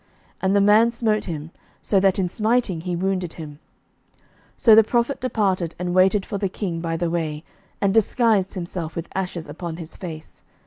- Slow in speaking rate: No, average, 185 wpm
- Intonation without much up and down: No, average, 3.8 semitones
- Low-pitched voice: No, medium, 185 Hz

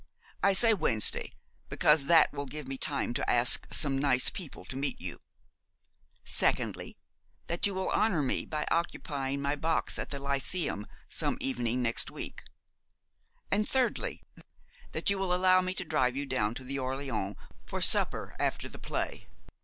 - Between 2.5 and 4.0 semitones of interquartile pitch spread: No, average, 5.3 semitones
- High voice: No, medium, 140 Hz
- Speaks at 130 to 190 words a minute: Yes, average, 160 wpm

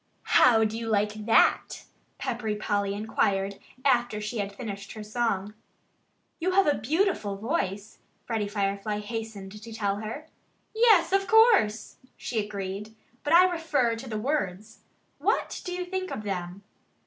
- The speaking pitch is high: Yes, high, 220 Hz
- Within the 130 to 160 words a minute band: Yes, average, 150 wpm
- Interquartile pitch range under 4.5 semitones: No, wide, 5.4 semitones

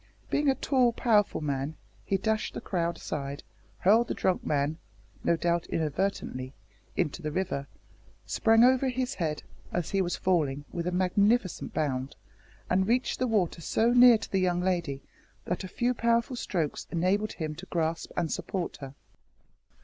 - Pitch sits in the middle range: Yes, medium, 180 Hz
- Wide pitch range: Yes, wide, 5.8 semitones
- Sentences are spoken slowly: No, average, 165 wpm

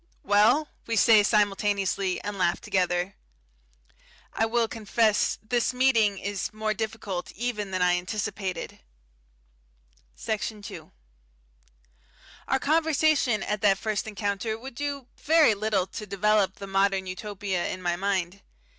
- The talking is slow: Yes, slow, 125 wpm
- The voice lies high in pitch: Yes, high, 210 Hz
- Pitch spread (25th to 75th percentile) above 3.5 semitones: No, narrow, 2.6 semitones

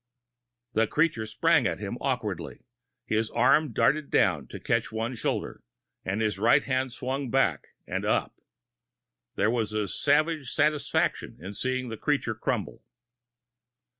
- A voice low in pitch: Yes, low, 120 Hz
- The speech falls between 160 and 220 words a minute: No, slow, 135 wpm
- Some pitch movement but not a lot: Yes, average, 4.6 semitones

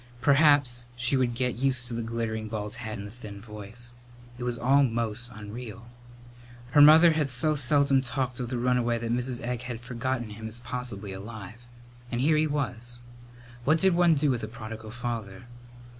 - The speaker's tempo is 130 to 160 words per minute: No, average, 185 wpm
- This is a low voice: Yes, low, 120 Hz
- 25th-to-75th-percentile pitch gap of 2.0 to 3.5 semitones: Yes, average, 2.7 semitones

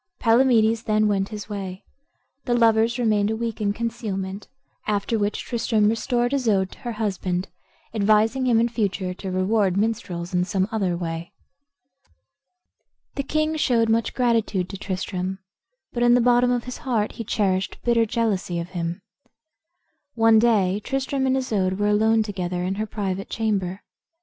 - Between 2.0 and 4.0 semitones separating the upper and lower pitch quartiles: Yes, average, 3.5 semitones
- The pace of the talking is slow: No, average, 155 wpm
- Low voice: No, high, 215 Hz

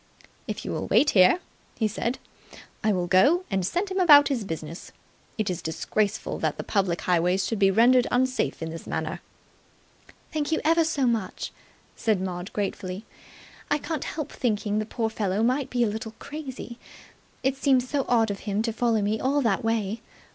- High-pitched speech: Yes, high, 225 Hz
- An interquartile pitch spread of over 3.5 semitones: Yes, average, 5.3 semitones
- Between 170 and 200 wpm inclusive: Yes, average, 185 wpm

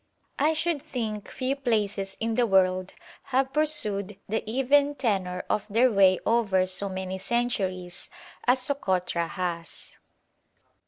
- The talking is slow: Yes, slow, 125 wpm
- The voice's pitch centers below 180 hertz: No, high, 210 Hz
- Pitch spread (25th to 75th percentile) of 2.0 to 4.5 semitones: No, wide, 5.5 semitones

